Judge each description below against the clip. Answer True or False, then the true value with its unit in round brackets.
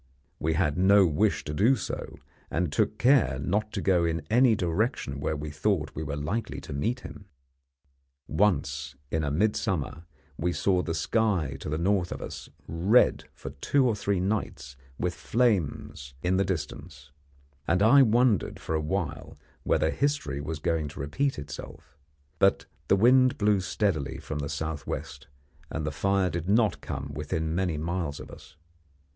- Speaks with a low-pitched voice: True (85 Hz)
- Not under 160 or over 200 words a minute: True (165 wpm)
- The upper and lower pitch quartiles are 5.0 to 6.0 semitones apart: True (5.6 semitones)